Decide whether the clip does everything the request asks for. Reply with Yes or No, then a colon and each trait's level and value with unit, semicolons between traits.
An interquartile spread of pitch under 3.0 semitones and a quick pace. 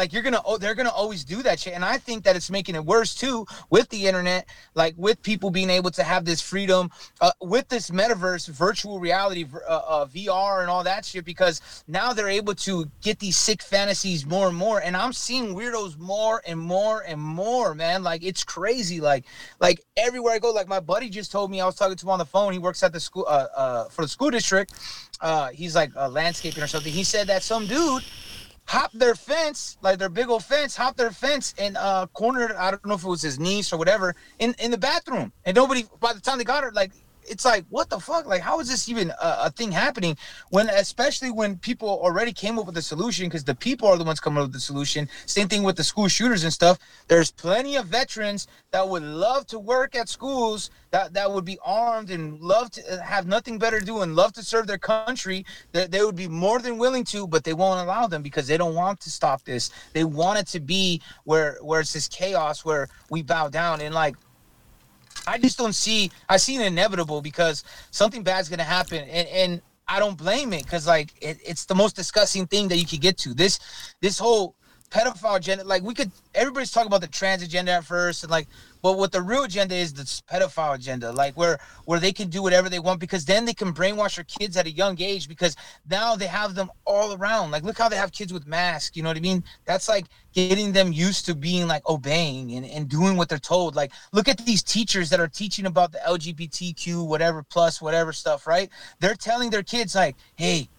No: average, 4.3 semitones; fast, 235 wpm